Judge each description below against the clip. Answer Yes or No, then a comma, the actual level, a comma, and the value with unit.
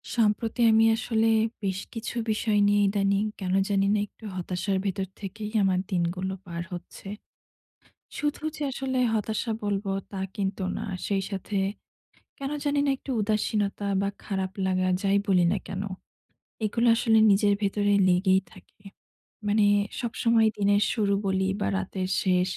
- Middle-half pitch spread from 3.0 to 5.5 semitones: No, narrow, 2.4 semitones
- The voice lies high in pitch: Yes, high, 200 Hz